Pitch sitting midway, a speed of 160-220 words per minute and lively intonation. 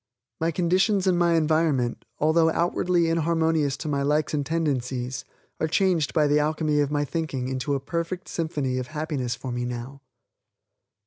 No: medium, 155 Hz; average, 165 wpm; average, 3.3 semitones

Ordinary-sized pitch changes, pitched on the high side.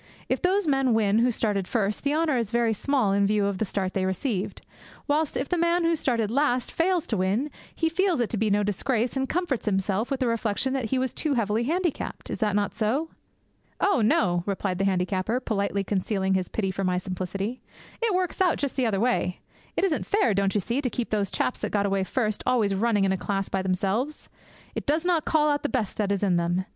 No: wide, 6.0 semitones; high, 225 Hz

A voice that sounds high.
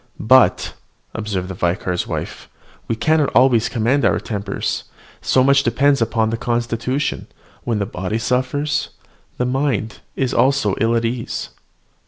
No: low, 120 Hz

